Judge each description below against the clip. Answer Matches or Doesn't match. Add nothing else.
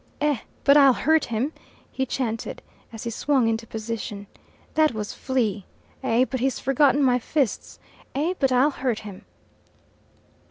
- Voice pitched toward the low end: Doesn't match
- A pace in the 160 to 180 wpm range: Doesn't match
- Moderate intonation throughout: Matches